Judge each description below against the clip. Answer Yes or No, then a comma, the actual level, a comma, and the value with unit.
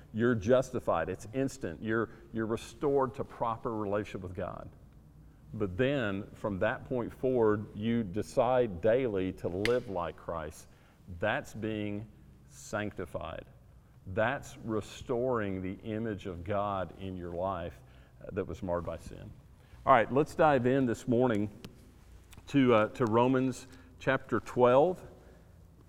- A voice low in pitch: Yes, low, 110 Hz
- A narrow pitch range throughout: No, average, 3.9 semitones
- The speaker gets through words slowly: Yes, slow, 125 wpm